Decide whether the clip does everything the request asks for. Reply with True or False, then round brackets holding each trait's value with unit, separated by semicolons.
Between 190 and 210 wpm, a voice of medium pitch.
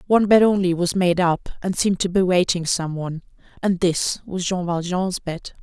True (205 wpm; 180 Hz)